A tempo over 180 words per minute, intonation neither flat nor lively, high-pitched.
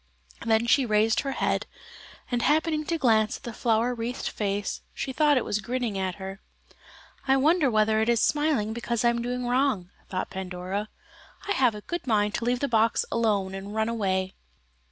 Yes: average, 190 wpm; average, 3.4 semitones; high, 230 Hz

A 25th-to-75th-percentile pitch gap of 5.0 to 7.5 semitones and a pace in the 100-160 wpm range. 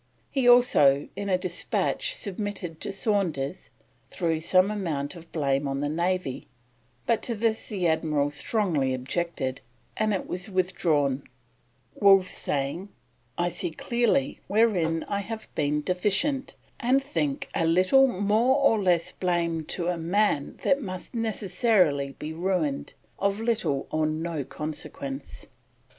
Yes: wide, 5.4 semitones; slow, 135 wpm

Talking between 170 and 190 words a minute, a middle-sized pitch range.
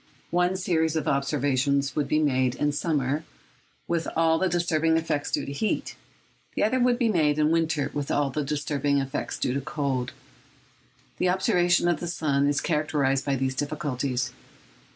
Yes: average, 175 wpm; average, 3.0 semitones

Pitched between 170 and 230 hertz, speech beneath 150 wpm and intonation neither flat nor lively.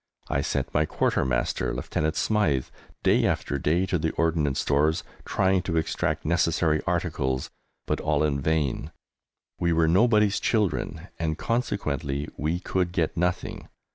No: very low, 80 Hz; average, 140 wpm; average, 3.4 semitones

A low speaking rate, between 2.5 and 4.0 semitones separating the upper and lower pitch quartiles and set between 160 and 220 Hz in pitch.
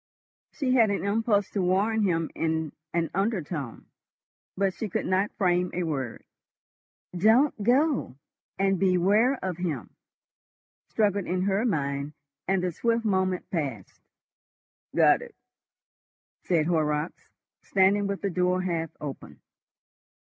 Yes: slow, 125 wpm; average, 3.7 semitones; medium, 185 Hz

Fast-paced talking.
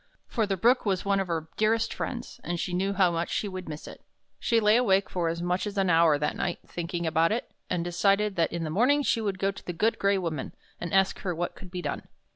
Yes: fast, 255 wpm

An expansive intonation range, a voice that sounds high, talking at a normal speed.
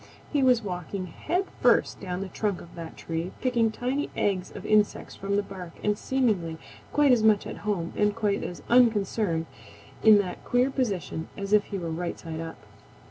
No: average, 4.3 semitones; high, 205 Hz; average, 190 wpm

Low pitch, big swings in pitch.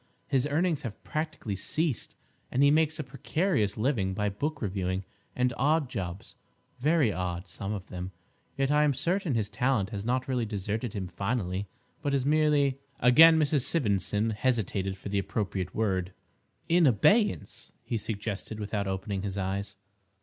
Yes: low, 110 Hz; wide, 6.4 semitones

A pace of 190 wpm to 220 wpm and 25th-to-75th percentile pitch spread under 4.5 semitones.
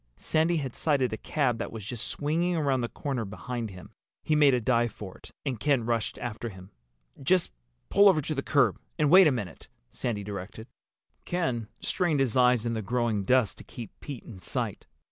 No: average, 200 wpm; average, 4.9 semitones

